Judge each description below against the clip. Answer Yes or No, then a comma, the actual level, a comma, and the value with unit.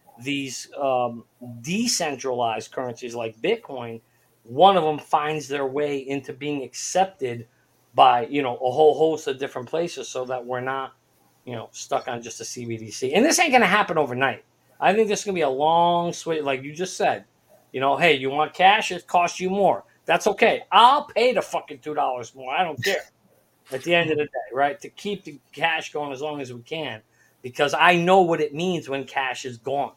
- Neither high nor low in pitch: Yes, medium, 145 Hz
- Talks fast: Yes, fast, 210 wpm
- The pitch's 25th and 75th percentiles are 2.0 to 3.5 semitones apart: No, average, 5.1 semitones